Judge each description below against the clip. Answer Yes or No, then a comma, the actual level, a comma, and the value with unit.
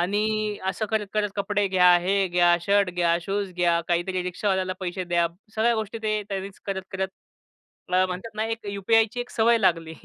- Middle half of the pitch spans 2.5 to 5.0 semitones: Yes, average, 2.8 semitones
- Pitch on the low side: No, high, 190 Hz